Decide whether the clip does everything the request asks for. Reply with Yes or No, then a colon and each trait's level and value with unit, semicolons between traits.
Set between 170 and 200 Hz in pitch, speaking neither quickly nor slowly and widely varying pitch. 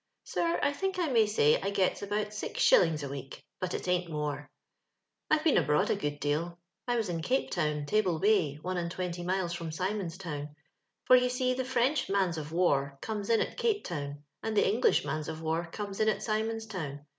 No: medium, 185 Hz; fast, 215 wpm; wide, 5.9 semitones